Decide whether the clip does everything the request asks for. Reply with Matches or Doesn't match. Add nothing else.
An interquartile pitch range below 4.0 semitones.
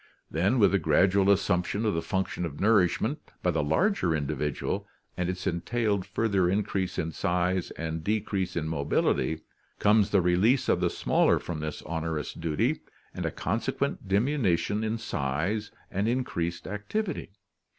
Doesn't match